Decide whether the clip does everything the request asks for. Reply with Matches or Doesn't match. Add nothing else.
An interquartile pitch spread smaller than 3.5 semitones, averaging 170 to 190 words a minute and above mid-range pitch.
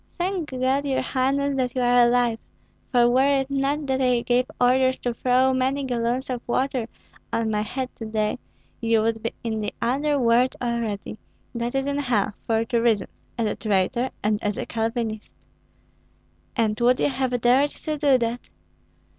Matches